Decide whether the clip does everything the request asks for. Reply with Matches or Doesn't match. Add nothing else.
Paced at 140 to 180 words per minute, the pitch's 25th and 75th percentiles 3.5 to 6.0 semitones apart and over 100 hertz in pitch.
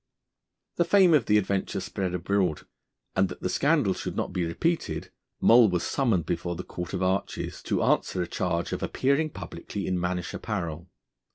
Doesn't match